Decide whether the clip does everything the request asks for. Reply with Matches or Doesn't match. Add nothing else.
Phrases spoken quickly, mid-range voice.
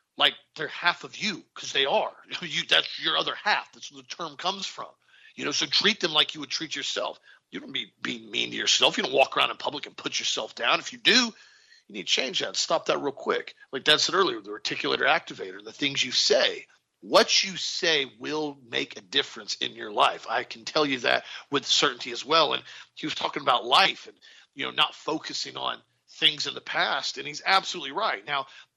Matches